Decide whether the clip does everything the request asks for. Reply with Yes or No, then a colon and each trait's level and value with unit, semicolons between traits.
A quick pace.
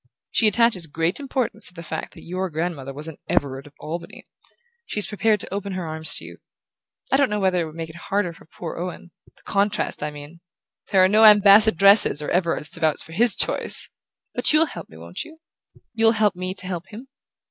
Yes: fast, 210 wpm